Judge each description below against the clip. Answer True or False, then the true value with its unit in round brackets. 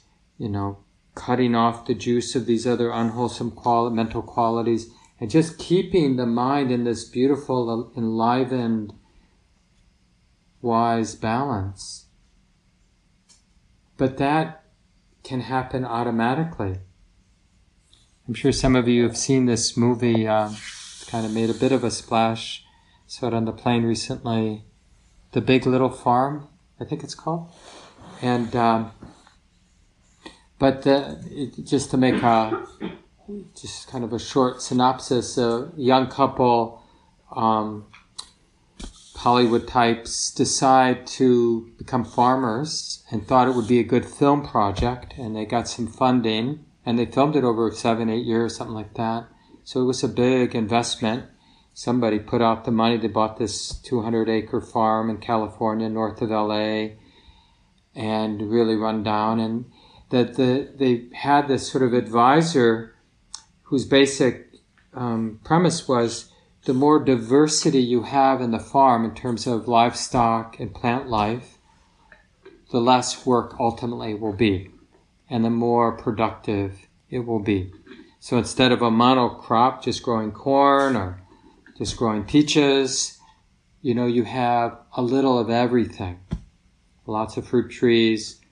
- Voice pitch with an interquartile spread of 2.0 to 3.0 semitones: True (2.4 semitones)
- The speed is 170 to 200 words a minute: False (140 wpm)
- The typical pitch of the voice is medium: False (120 Hz)